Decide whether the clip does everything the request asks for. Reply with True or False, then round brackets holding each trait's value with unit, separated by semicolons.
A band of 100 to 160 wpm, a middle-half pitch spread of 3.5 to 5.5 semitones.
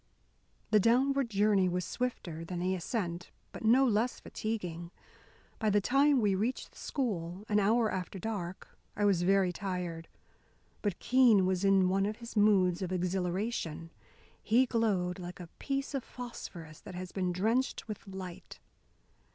True (155 wpm; 4.0 semitones)